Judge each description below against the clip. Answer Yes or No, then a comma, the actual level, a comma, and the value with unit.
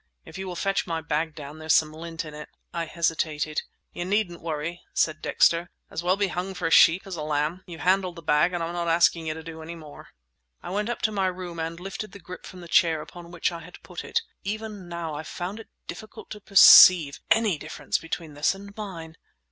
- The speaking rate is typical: No, fast, 230 wpm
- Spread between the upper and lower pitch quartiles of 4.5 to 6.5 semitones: No, narrow, 2.6 semitones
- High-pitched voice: No, medium, 170 Hz